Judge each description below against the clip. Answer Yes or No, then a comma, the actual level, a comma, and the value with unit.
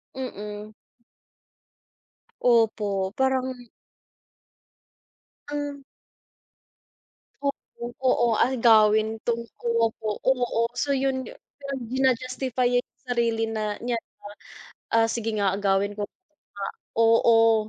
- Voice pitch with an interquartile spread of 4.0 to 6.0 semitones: No, average, 2.9 semitones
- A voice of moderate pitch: No, high, 230 Hz